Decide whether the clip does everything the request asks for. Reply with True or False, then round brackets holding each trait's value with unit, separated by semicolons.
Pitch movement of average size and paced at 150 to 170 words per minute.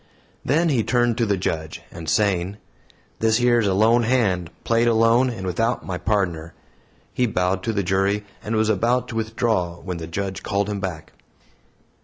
False (3.9 semitones; 180 wpm)